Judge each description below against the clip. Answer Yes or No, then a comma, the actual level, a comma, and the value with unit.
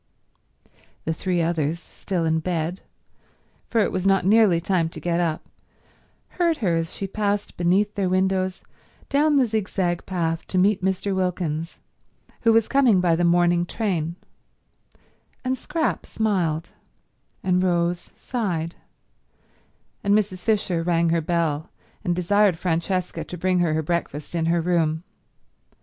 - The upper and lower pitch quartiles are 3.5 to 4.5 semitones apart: No, average, 3.0 semitones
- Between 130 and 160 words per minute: Yes, average, 140 wpm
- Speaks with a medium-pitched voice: Yes, medium, 180 Hz